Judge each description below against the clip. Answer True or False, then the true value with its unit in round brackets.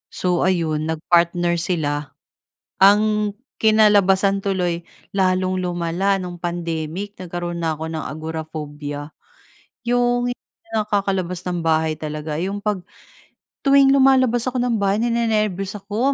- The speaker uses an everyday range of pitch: True (4.2 semitones)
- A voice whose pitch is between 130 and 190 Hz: True (185 Hz)